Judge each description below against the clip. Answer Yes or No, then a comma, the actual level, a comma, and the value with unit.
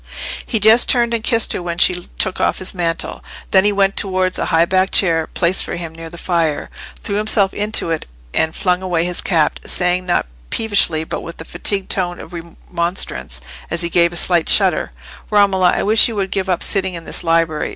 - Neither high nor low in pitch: Yes, medium, 180 Hz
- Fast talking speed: Yes, fast, 210 wpm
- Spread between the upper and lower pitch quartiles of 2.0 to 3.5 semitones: Yes, narrow, 2.6 semitones